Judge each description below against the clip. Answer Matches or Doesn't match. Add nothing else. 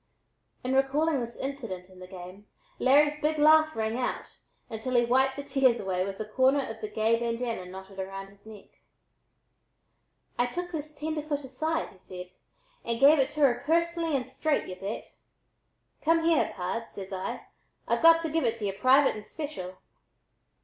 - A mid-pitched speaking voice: Doesn't match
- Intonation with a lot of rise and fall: Matches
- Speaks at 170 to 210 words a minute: Matches